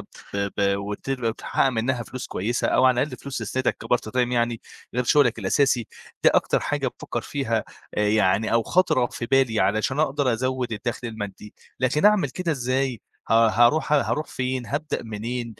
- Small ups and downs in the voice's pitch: No, average, 3.2 semitones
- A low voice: Yes, low, 120 Hz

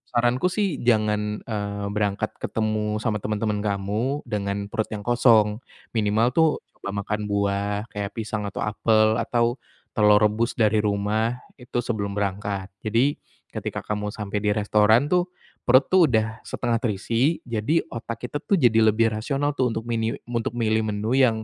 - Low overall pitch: Yes, low, 110 Hz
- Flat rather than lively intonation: Yes, narrow, 2.3 semitones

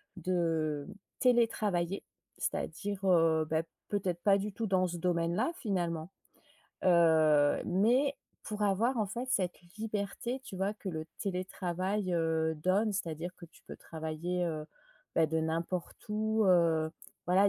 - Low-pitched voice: No, medium, 180 Hz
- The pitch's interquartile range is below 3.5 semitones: No, average, 3.8 semitones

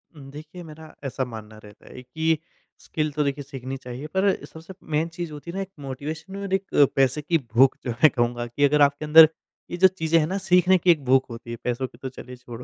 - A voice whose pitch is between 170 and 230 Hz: No, medium, 145 Hz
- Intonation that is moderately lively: Yes, average, 4.1 semitones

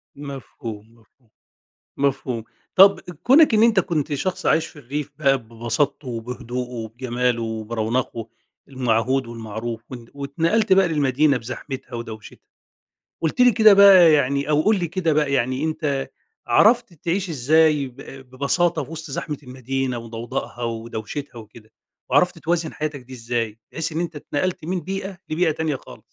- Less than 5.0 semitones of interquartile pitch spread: No, average, 5.3 semitones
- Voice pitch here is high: No, medium, 140 Hz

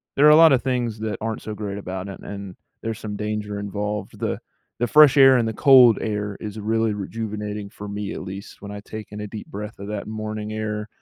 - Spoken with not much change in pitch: Yes, narrow, 1.6 semitones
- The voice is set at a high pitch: No, low, 105 Hz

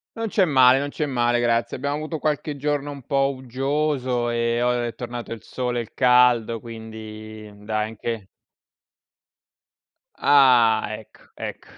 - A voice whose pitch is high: No, low, 120 Hz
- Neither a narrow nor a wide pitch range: Yes, average, 3.3 semitones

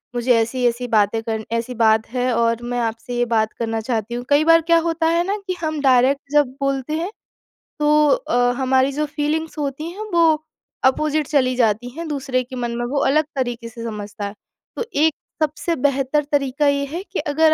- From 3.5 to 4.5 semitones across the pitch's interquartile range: Yes, average, 4.1 semitones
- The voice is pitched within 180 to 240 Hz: No, very high, 265 Hz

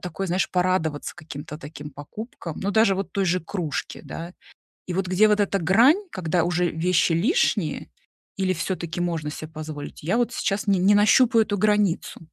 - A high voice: No, medium, 180 Hz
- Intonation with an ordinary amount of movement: Yes, average, 3.9 semitones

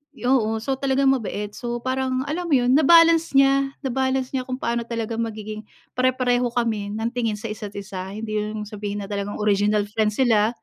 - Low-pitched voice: No, high, 235 Hz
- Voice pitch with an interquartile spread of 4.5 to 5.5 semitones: No, average, 3.8 semitones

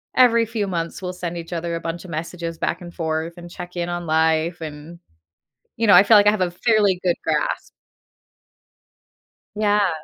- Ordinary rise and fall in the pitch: Yes, average, 3.1 semitones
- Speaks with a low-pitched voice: No, medium, 175 Hz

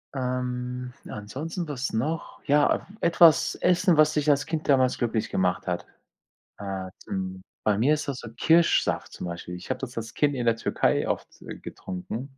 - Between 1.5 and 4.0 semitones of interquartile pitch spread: No, wide, 5.6 semitones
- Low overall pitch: Yes, low, 125 Hz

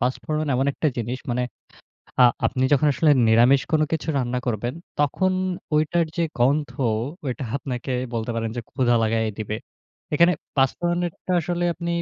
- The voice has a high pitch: No, low, 135 Hz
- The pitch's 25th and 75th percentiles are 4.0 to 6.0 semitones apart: Yes, average, 4.5 semitones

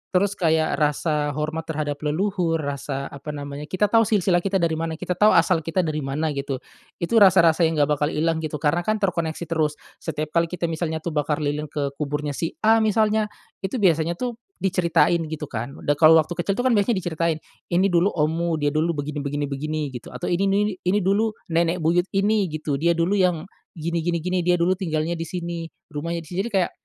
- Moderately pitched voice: Yes, medium, 165 Hz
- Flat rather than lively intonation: No, average, 3.1 semitones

